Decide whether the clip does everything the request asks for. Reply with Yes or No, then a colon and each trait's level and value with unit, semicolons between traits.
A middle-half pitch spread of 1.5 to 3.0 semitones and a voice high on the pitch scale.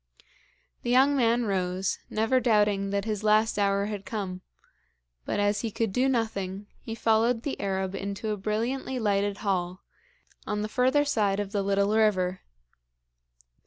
Yes: narrow, 2.5 semitones; high, 210 Hz